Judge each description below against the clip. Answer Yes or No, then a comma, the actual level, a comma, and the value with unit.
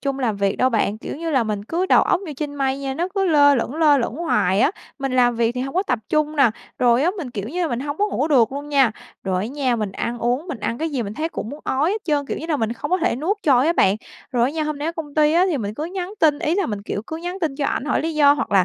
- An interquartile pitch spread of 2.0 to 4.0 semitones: No, average, 5.0 semitones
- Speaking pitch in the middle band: No, very high, 285 Hz